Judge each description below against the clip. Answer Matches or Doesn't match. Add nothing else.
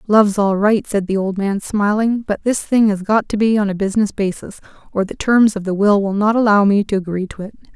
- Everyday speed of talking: Doesn't match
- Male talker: Doesn't match